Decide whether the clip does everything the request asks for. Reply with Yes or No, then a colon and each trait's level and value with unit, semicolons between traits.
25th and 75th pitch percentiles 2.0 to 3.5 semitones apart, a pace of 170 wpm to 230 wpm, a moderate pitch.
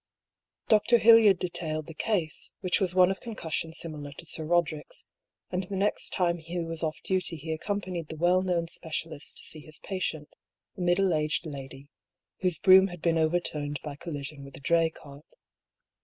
Yes: average, 3.0 semitones; average, 175 wpm; medium, 165 Hz